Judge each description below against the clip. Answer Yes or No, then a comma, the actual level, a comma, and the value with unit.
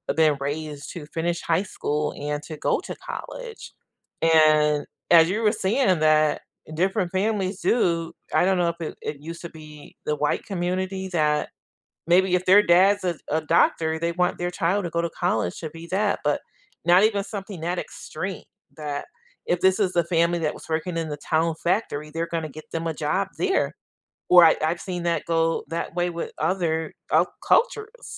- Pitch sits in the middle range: Yes, medium, 170 Hz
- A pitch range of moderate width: Yes, average, 3.0 semitones